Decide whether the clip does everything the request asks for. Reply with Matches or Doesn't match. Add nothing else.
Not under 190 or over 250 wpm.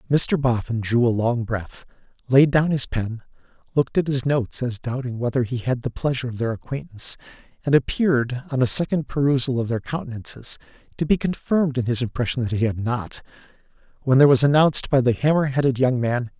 Matches